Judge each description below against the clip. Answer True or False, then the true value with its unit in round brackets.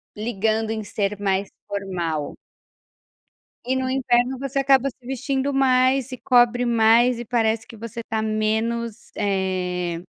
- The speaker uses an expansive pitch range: False (3.8 semitones)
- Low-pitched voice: False (230 Hz)